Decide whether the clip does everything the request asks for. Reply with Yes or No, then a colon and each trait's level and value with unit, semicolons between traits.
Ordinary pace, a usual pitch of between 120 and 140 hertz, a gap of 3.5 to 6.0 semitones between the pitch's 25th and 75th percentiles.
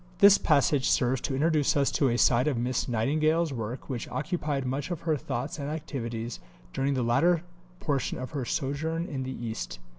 Yes: average, 185 wpm; low, 135 Hz; average, 3.8 semitones